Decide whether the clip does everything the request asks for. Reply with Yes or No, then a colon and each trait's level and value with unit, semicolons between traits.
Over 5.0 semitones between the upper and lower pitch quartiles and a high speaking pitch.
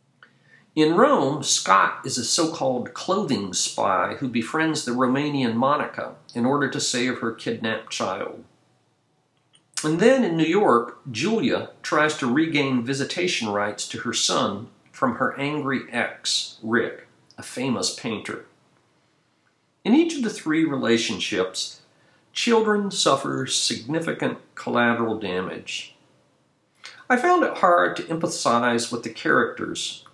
No: wide, 5.5 semitones; medium, 140 Hz